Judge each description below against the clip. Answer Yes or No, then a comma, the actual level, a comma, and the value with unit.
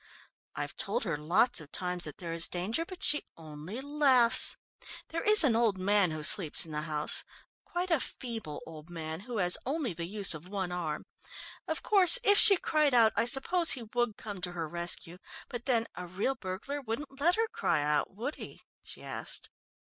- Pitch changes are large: Yes, wide, 8.1 semitones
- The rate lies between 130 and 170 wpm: No, average, 195 wpm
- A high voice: Yes, high, 205 Hz